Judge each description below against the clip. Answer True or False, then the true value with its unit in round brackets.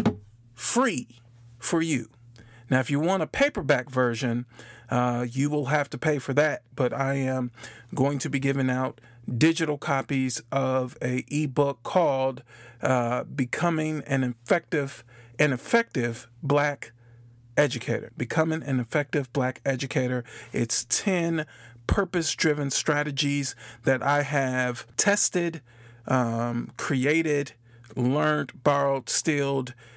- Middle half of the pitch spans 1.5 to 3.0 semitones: False (3.5 semitones)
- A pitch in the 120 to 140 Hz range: True (135 Hz)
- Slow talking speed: True (115 wpm)